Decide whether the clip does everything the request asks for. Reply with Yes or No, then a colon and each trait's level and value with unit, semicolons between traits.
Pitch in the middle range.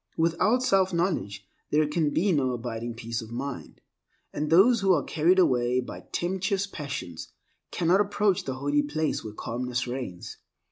Yes: medium, 150 Hz